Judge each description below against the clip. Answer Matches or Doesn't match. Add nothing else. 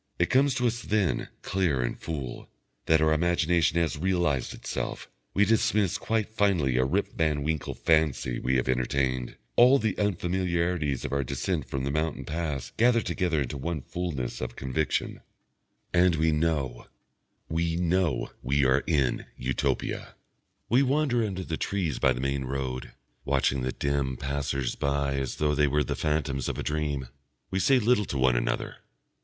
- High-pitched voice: Doesn't match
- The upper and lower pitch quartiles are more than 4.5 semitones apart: Matches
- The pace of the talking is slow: Doesn't match